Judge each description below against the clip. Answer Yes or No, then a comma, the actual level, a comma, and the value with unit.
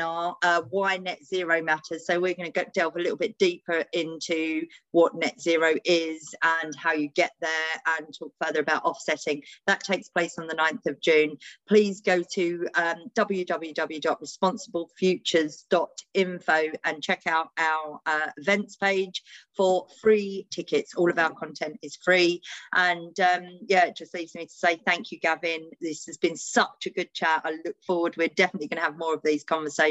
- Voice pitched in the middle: Yes, medium, 170 Hz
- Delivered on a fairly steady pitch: Yes, narrow, 2.2 semitones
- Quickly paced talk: No, average, 180 wpm